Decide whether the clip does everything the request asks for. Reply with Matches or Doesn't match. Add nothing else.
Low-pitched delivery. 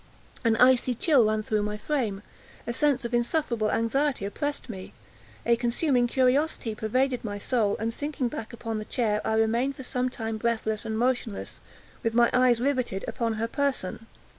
Doesn't match